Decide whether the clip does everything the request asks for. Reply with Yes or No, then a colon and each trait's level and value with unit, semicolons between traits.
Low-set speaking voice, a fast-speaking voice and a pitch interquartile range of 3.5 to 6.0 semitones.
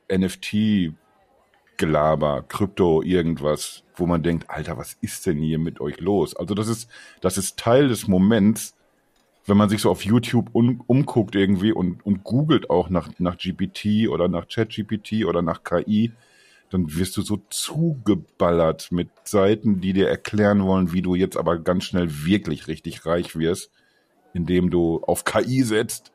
No: very low, 95 Hz; average, 160 wpm; average, 3.8 semitones